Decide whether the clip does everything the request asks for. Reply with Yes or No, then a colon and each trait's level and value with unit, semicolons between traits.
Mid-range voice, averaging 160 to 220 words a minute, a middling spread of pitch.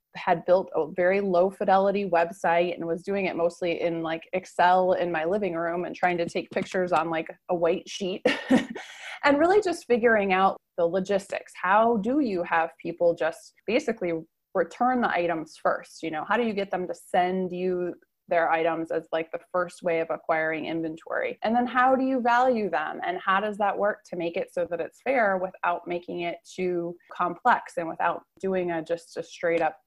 Yes: medium, 180 Hz; average, 200 wpm; average, 3.5 semitones